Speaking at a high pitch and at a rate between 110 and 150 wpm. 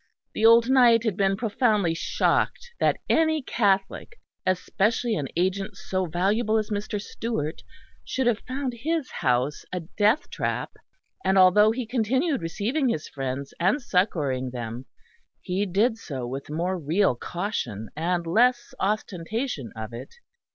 Yes: high, 200 Hz; average, 140 wpm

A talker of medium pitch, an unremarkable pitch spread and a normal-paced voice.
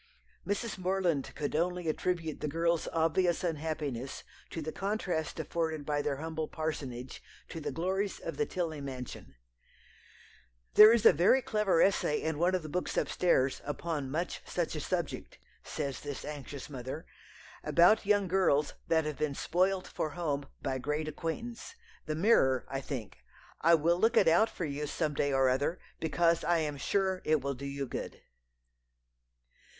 Yes: medium, 160 Hz; average, 3.9 semitones; average, 165 wpm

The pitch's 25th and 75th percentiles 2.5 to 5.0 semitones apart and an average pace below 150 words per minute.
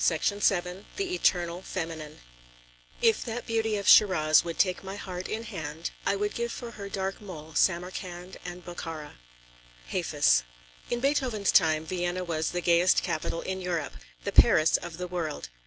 No: average, 3.6 semitones; average, 160 wpm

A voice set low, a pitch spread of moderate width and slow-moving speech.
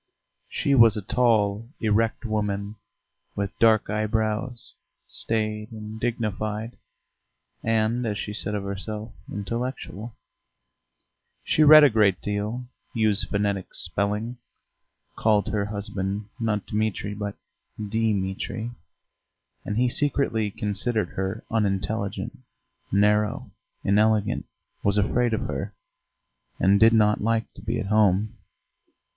No: low, 105 Hz; narrow, 1.7 semitones; slow, 110 wpm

